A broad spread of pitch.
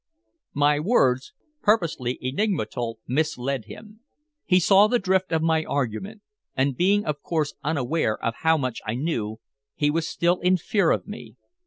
Yes: wide, 6.3 semitones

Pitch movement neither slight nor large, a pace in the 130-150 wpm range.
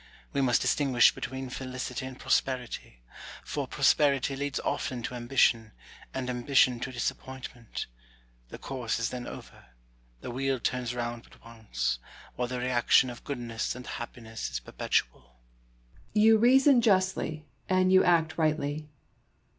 Yes: average, 3.2 semitones; average, 145 wpm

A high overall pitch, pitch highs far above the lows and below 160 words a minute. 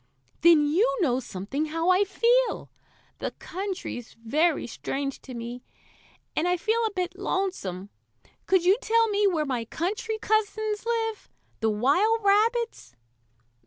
Yes: very high, 365 Hz; wide, 7.8 semitones; slow, 135 wpm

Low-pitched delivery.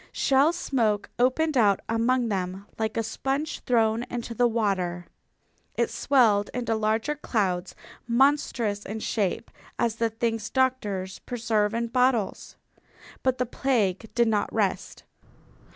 No: high, 230 Hz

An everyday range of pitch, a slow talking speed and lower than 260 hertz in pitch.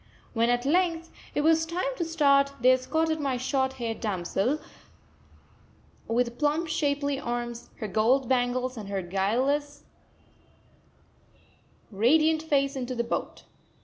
No: average, 4.1 semitones; slow, 125 wpm; very high, 265 Hz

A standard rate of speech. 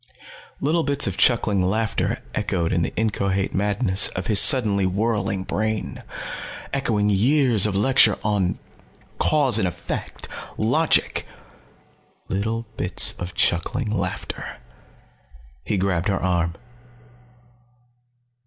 No: slow, 105 wpm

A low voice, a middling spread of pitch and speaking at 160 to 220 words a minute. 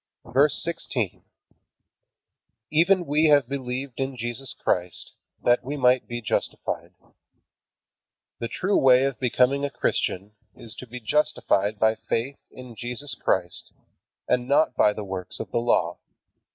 No: low, 125 Hz; average, 3.6 semitones; average, 140 wpm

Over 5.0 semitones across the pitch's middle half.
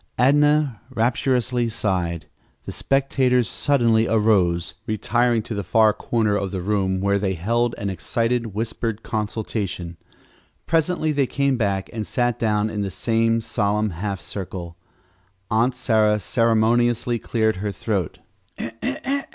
No: average, 3.2 semitones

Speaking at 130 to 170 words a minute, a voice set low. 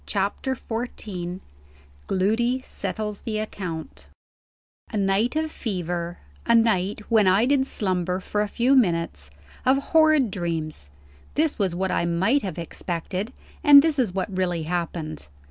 No: average, 140 wpm; high, 195 Hz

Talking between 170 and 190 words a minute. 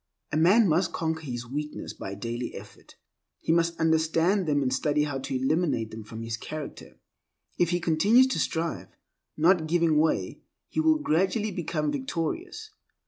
No: average, 160 wpm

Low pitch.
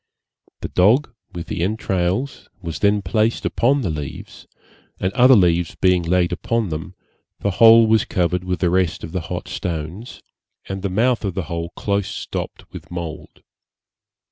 Yes: very low, 95 Hz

